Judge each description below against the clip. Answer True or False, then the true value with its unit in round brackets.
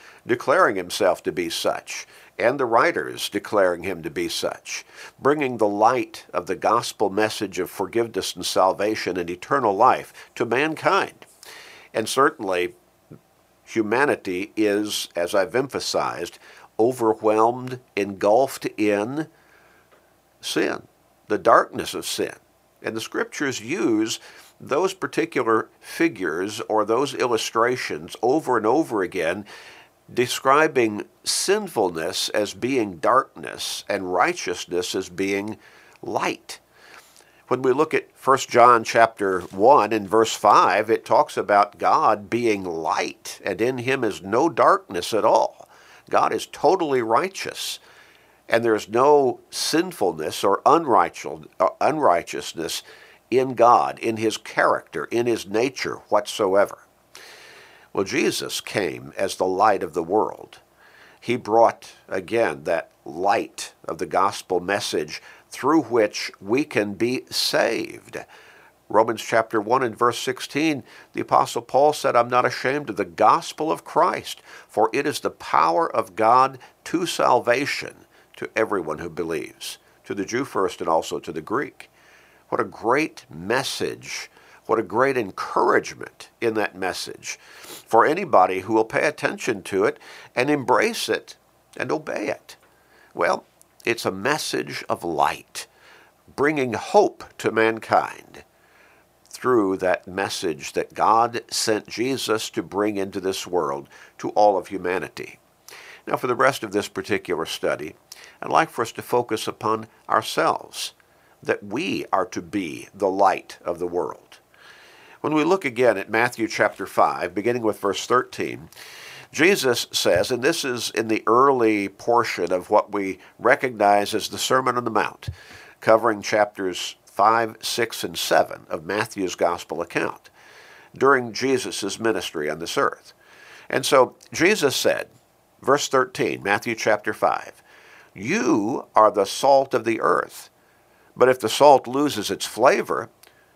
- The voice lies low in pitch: True (115 Hz)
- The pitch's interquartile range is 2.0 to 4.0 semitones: False (4.7 semitones)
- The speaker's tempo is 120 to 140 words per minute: True (135 wpm)